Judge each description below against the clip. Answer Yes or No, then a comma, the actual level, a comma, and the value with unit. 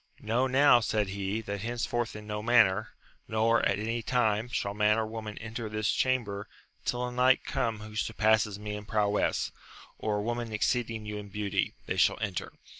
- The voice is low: Yes, low, 110 Hz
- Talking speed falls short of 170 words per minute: No, average, 185 wpm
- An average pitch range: No, narrow, 2.1 semitones